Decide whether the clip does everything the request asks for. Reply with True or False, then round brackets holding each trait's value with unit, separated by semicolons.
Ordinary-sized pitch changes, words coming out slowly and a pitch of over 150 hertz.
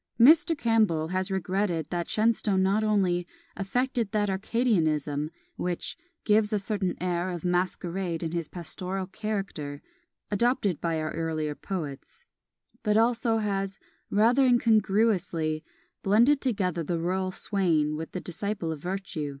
True (4.2 semitones; 130 wpm; 190 Hz)